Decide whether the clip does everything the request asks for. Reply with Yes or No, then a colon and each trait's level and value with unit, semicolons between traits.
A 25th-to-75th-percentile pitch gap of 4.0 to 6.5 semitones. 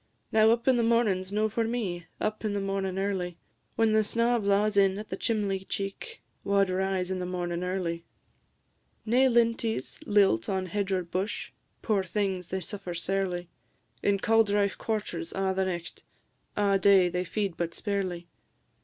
No: narrow, 2.6 semitones